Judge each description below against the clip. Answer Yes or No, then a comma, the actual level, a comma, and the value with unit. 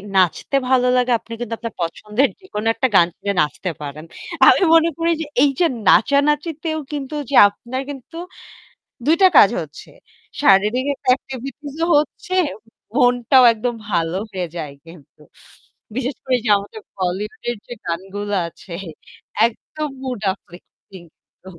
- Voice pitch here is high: Yes, high, 235 Hz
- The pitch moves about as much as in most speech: No, wide, 6.5 semitones